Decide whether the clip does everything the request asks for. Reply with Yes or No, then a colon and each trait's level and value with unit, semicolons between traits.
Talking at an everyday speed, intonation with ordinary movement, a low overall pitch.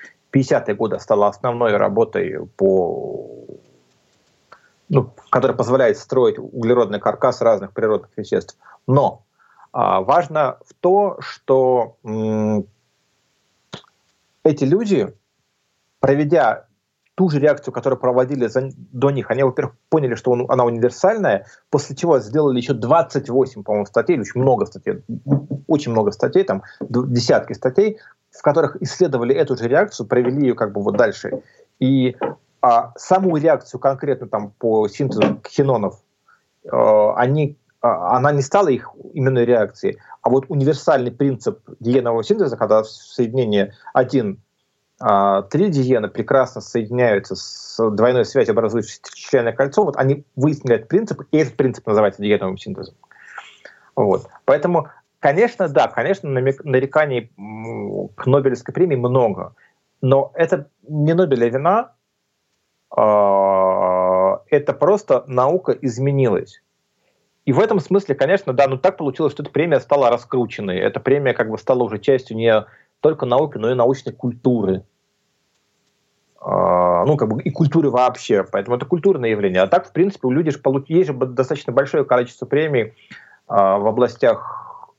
Yes: average, 130 wpm; average, 4.0 semitones; low, 130 Hz